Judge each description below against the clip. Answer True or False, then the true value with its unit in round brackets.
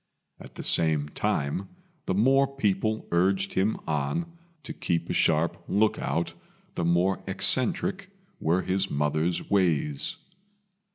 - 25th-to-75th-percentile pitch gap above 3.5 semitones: True (4.6 semitones)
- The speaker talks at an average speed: False (125 wpm)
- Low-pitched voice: True (95 Hz)